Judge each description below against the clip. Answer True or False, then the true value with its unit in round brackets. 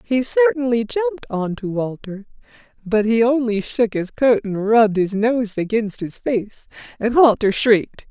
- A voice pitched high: True (230 Hz)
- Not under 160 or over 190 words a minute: True (165 wpm)